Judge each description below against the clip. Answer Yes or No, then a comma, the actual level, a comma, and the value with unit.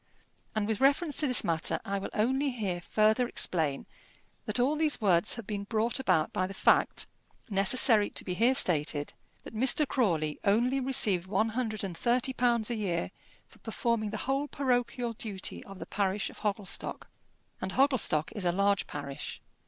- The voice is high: Yes, high, 215 Hz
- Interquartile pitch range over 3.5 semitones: Yes, average, 4.7 semitones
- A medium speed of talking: Yes, average, 175 wpm